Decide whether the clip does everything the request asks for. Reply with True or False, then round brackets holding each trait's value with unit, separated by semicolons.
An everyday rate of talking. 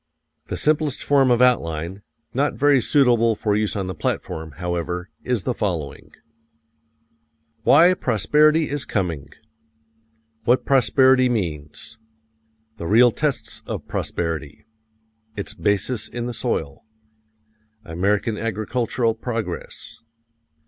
False (105 wpm)